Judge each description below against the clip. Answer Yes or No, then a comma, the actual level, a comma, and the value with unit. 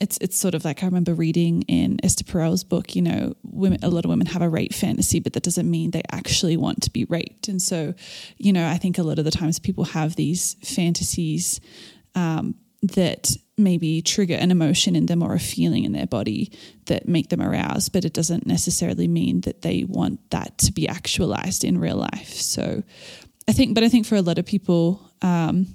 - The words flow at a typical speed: No, fast, 215 wpm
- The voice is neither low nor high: Yes, medium, 175 Hz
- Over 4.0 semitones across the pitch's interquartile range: No, narrow, 2.6 semitones